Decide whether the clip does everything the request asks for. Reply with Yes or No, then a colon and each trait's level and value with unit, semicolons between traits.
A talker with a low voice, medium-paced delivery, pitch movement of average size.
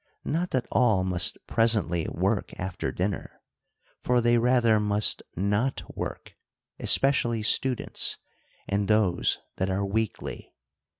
No: low, 110 Hz; slow, 120 wpm; average, 3.6 semitones